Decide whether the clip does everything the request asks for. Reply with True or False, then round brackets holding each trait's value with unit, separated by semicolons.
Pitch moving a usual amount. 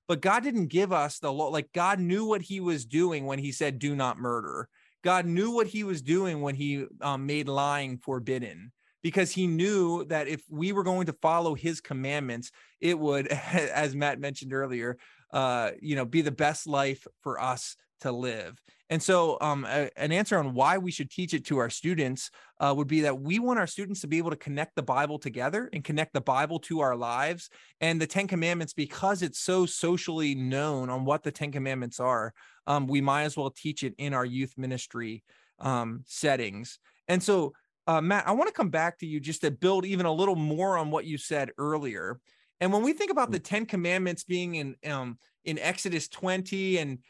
True (4.5 semitones)